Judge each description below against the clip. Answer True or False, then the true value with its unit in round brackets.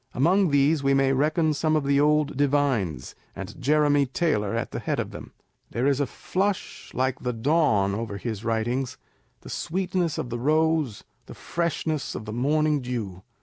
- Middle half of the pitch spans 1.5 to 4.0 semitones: False (4.4 semitones)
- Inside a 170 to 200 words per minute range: True (175 wpm)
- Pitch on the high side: False (140 Hz)